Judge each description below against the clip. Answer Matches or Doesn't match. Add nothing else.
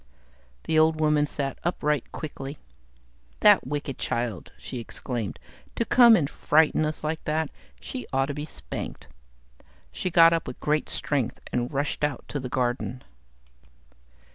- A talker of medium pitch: Matches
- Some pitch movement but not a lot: Matches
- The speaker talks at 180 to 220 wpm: Doesn't match